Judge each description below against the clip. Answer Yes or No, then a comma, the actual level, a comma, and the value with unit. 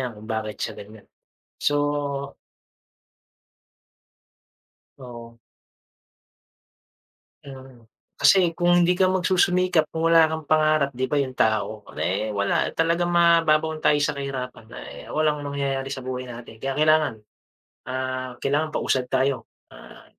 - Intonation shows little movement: No, average, 3.8 semitones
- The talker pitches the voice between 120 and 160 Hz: Yes, medium, 140 Hz